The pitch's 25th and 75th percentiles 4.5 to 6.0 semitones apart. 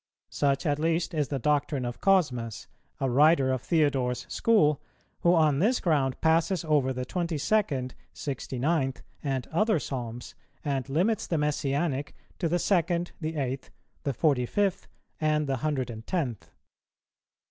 No: average, 3.9 semitones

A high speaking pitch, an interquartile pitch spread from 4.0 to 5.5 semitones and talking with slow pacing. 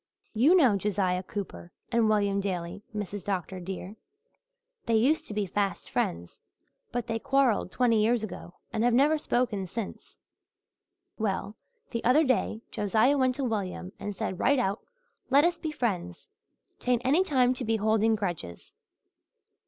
No: high, 220 Hz; average, 4.3 semitones; average, 155 wpm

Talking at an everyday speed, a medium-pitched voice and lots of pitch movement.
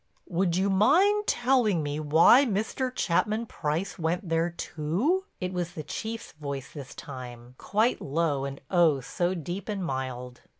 Yes: average, 155 wpm; medium, 175 Hz; wide, 6.3 semitones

